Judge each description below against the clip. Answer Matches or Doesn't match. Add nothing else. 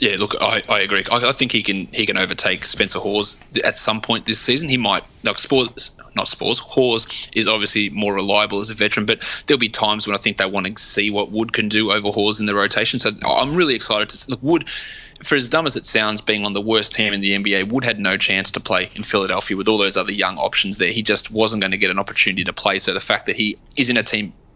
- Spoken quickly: Matches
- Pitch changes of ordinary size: Doesn't match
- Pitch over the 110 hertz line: Doesn't match